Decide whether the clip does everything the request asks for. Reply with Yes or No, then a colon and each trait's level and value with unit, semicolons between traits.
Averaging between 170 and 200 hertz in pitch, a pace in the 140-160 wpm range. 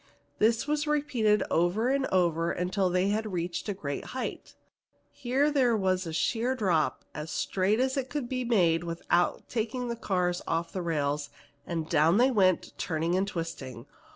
No: high, 190 Hz; average, 170 wpm